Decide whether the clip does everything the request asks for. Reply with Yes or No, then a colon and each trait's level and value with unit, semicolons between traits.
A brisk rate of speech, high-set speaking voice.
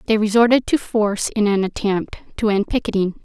No: average, 185 wpm; high, 210 Hz